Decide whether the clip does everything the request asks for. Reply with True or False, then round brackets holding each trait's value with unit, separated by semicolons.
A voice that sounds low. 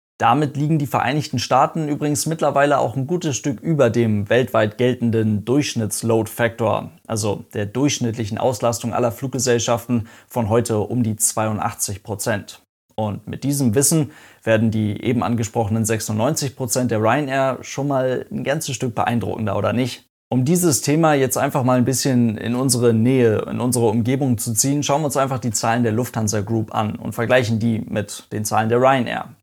True (120 Hz)